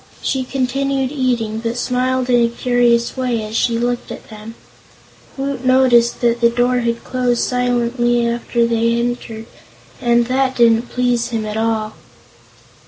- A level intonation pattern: Yes, narrow, 1.3 semitones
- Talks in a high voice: Yes, high, 240 Hz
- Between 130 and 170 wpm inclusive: Yes, average, 155 wpm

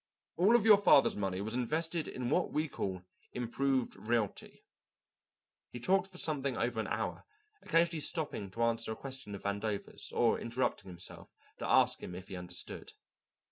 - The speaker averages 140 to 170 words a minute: Yes, average, 165 wpm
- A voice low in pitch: Yes, low, 120 Hz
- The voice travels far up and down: Yes, wide, 7.2 semitones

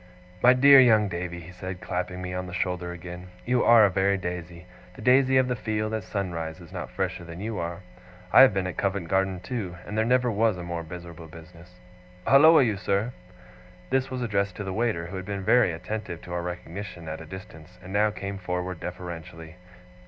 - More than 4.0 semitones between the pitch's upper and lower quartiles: No, average, 3.6 semitones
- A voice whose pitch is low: Yes, very low, 95 Hz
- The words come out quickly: Yes, fast, 210 wpm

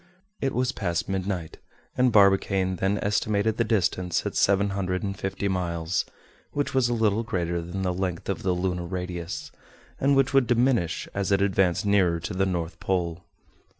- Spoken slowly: No, average, 175 wpm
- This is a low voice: Yes, very low, 95 Hz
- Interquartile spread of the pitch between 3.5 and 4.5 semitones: No, average, 2.7 semitones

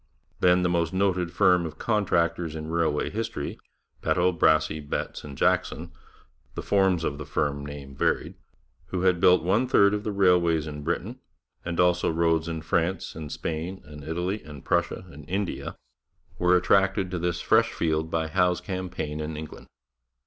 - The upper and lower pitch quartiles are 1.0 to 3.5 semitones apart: Yes, average, 2.8 semitones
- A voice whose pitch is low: Yes, very low, 85 Hz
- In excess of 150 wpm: Yes, average, 165 wpm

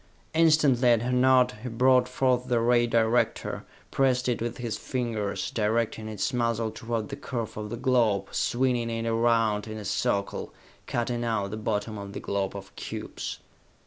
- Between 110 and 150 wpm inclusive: No, average, 170 wpm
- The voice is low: Yes, low, 115 Hz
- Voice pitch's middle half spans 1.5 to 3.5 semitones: Yes, narrow, 2.4 semitones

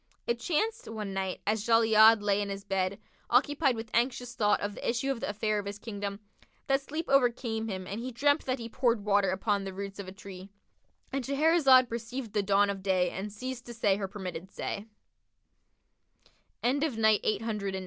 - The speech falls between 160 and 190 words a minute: Yes, average, 180 wpm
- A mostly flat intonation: No, average, 3.7 semitones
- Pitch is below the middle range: No, high, 220 Hz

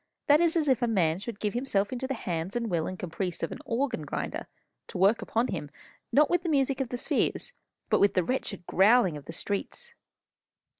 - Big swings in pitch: Yes, wide, 6.4 semitones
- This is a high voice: Yes, high, 225 Hz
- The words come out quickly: Yes, fast, 215 wpm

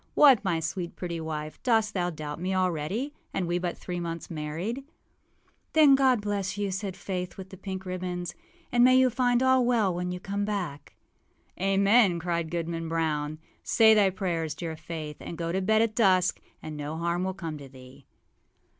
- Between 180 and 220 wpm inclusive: Yes, average, 185 wpm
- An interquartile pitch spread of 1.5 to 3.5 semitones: No, average, 3.9 semitones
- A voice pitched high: No, medium, 180 Hz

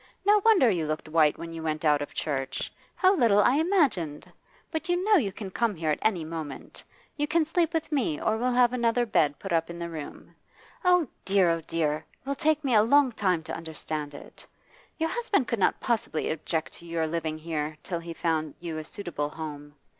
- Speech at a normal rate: No, fast, 215 wpm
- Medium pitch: Yes, medium, 175 Hz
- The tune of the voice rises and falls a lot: Yes, wide, 9.0 semitones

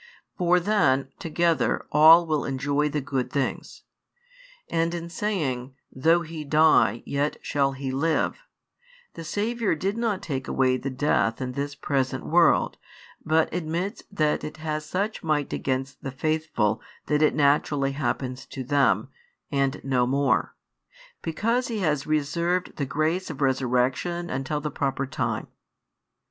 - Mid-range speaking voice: Yes, medium, 150 Hz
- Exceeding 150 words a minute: No, average, 140 wpm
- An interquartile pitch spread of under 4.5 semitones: Yes, average, 3.7 semitones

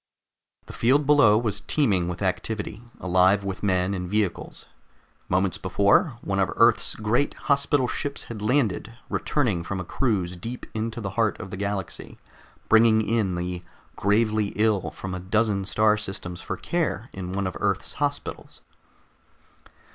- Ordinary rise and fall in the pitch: Yes, average, 3.5 semitones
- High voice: No, low, 105 Hz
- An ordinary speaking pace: Yes, average, 150 wpm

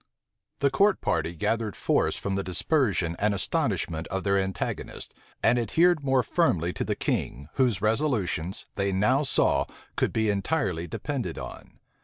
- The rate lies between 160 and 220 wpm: No, average, 150 wpm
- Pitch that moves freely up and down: Yes, wide, 6.5 semitones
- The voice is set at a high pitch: No, low, 100 Hz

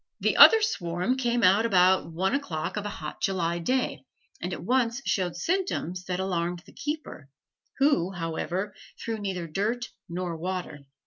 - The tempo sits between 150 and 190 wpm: Yes, average, 155 wpm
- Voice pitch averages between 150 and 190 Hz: Yes, medium, 185 Hz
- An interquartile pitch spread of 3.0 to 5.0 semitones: No, wide, 5.4 semitones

